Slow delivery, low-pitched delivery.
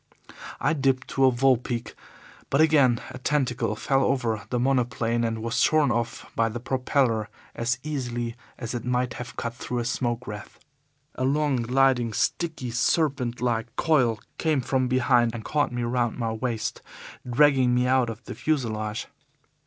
No: average, 165 wpm; low, 125 Hz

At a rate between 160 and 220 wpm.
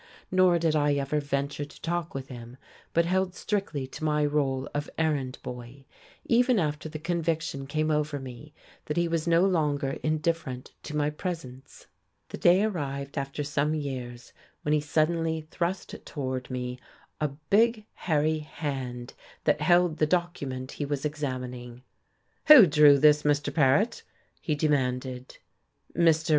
No: average, 150 wpm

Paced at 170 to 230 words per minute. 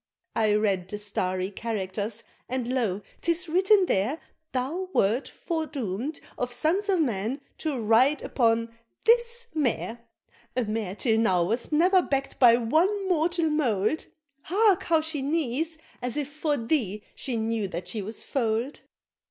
No: average, 150 wpm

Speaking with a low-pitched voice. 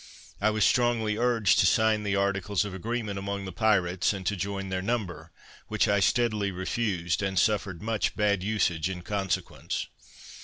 Yes: low, 100 Hz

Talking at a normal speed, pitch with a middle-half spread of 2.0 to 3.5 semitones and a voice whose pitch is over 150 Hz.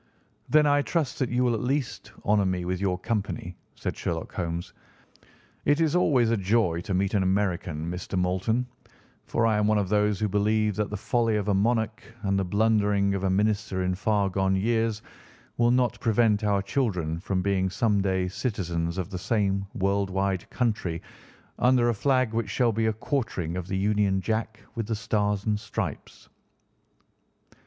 No: average, 180 wpm; average, 3.0 semitones; low, 105 Hz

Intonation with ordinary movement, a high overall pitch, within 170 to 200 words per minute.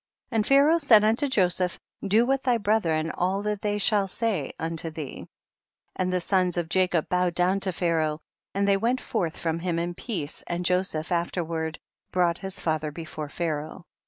No: average, 3.8 semitones; medium, 180 Hz; average, 180 wpm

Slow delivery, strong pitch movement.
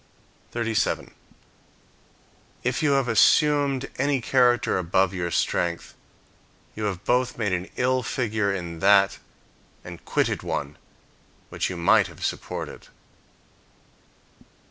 Yes: slow, 110 wpm; wide, 5.7 semitones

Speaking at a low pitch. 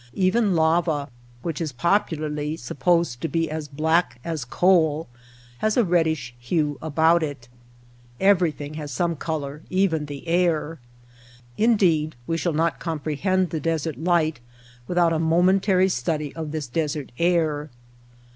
No: medium, 160 Hz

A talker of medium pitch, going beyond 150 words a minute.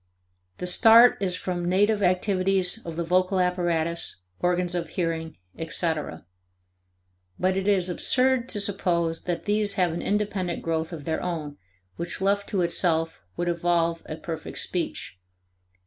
No: medium, 180 Hz; average, 145 wpm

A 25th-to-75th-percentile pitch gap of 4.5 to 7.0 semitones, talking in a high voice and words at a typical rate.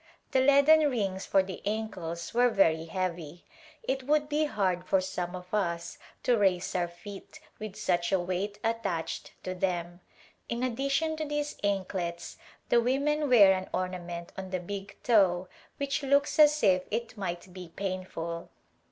Yes: wide, 5.6 semitones; high, 195 Hz; average, 160 wpm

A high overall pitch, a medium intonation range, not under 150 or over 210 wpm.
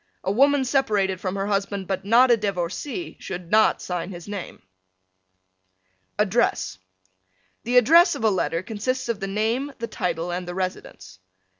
Yes: high, 200 Hz; average, 4.5 semitones; average, 155 wpm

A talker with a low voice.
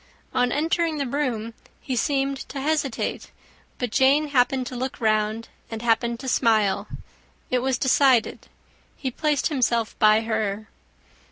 No: very high, 250 Hz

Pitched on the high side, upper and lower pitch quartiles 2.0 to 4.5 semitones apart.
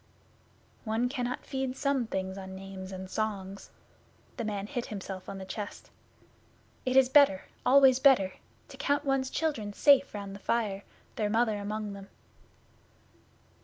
No: high, 215 Hz; average, 5.1 semitones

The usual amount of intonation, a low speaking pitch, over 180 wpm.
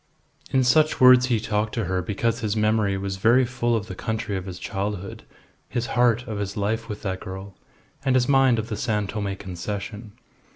Yes: average, 3.3 semitones; low, 110 Hz; average, 200 wpm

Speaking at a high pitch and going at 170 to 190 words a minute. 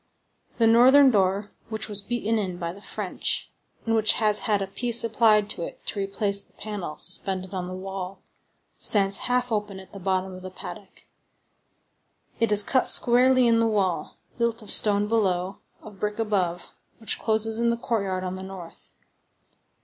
Yes: high, 205 Hz; average, 175 wpm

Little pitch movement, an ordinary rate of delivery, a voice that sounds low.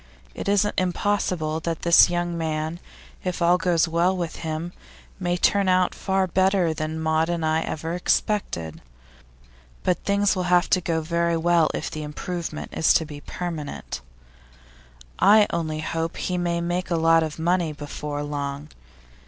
No: narrow, 2.3 semitones; average, 160 wpm; medium, 170 Hz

